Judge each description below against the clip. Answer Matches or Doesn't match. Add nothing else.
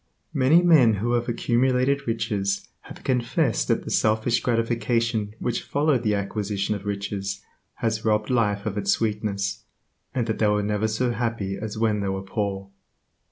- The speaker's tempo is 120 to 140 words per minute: Doesn't match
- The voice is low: Matches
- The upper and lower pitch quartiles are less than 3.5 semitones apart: Matches